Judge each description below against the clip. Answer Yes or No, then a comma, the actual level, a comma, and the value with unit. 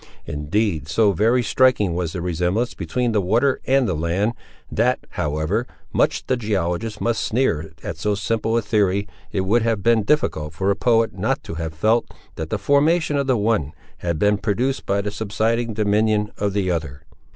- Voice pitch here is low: Yes, low, 105 Hz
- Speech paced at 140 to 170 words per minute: No, average, 185 wpm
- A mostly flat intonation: No, average, 4.6 semitones